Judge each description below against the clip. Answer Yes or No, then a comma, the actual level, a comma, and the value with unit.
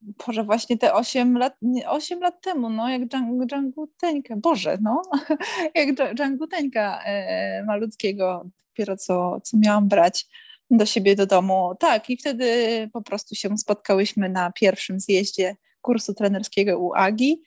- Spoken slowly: No, average, 150 wpm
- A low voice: No, high, 225 Hz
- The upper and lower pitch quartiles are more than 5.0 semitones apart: Yes, wide, 5.4 semitones